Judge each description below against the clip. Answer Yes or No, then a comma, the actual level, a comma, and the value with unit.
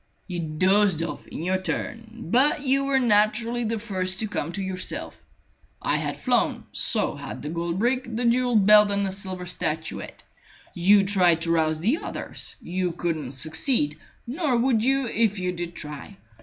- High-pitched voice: Yes, high, 195 Hz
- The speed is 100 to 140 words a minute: No, average, 170 wpm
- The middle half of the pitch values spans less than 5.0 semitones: No, wide, 5.5 semitones